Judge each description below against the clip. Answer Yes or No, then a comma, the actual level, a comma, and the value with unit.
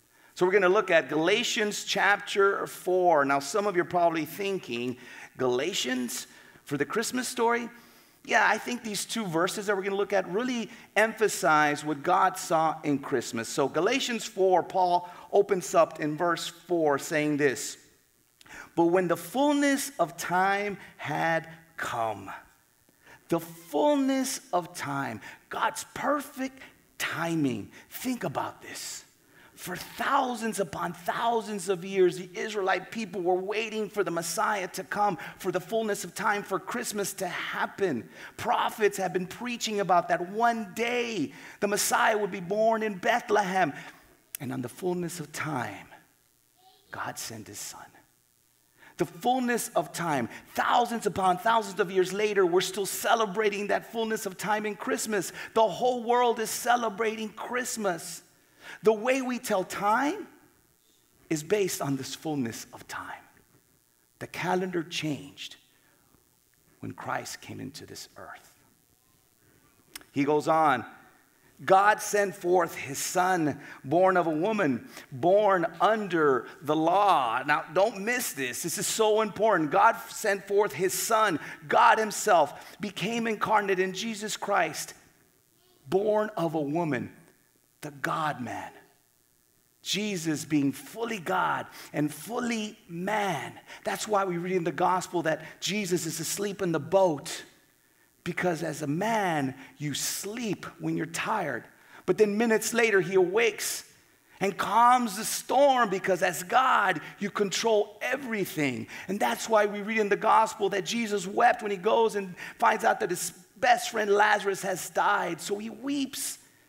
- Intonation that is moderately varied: Yes, average, 4.4 semitones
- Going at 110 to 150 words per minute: Yes, average, 145 wpm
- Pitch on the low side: No, high, 195 Hz